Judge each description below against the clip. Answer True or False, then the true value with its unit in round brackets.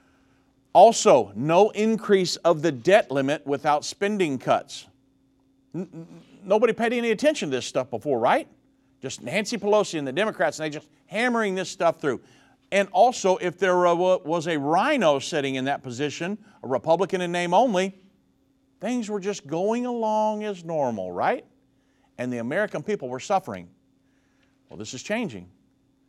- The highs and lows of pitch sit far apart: True (7.3 semitones)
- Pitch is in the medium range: True (175 Hz)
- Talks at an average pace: True (155 wpm)